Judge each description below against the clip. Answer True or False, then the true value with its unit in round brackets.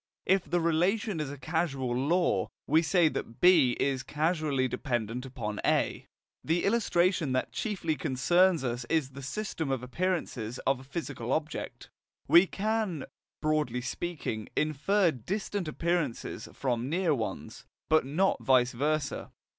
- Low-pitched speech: False (155 Hz)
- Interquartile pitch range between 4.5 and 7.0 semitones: True (5.2 semitones)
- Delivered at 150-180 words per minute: False (140 wpm)